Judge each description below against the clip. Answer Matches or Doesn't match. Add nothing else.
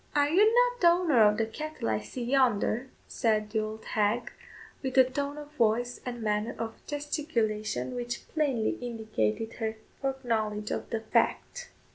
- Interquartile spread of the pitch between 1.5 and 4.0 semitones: Doesn't match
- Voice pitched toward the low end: Doesn't match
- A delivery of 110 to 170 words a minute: Matches